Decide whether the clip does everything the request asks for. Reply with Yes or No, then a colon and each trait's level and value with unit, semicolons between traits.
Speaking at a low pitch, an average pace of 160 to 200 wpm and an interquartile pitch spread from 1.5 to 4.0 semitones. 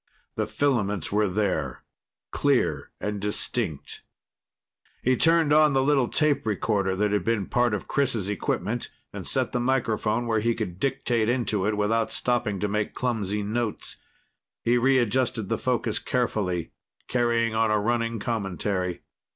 No: low, 110 Hz; average, 145 wpm; average, 2.9 semitones